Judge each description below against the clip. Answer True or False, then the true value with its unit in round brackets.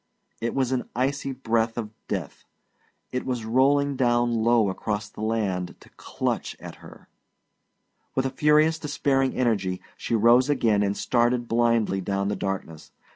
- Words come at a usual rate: True (150 wpm)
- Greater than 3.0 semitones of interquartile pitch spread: True (3.8 semitones)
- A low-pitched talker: True (120 Hz)